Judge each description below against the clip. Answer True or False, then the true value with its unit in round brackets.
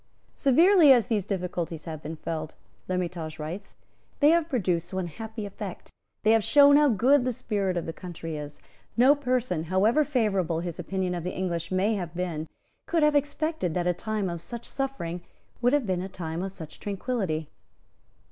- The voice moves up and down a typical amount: False (6.5 semitones)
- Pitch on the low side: False (190 Hz)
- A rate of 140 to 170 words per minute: False (180 wpm)